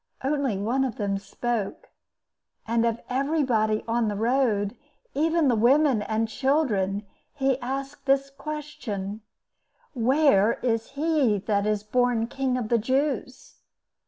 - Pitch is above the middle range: Yes, high, 245 Hz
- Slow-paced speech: Yes, slow, 125 wpm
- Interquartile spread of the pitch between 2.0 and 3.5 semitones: No, average, 4.2 semitones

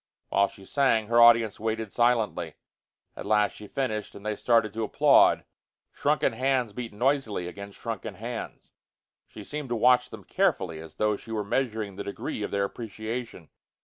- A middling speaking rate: Yes, average, 170 wpm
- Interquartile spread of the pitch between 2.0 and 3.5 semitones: Yes, average, 2.9 semitones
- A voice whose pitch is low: Yes, low, 110 Hz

